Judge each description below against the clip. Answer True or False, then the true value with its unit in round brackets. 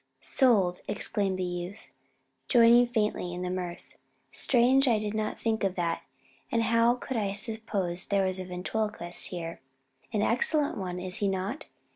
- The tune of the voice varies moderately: True (4.1 semitones)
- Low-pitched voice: False (205 Hz)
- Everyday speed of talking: True (160 wpm)